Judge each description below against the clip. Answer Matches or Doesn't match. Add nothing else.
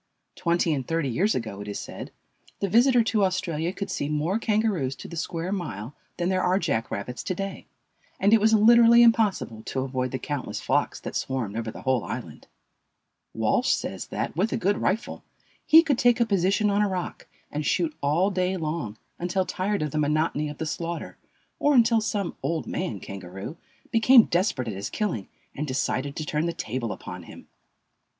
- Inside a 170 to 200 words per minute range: Matches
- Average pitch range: Doesn't match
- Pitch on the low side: Doesn't match